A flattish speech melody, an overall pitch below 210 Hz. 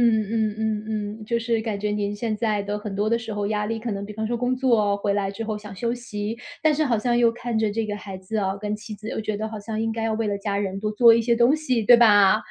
No: narrow, 1.9 semitones; high, 215 Hz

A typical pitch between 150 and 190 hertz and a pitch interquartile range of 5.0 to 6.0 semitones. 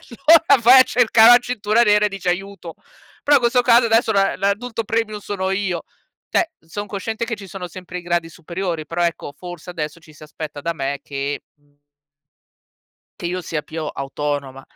Yes: medium, 185 Hz; wide, 5.5 semitones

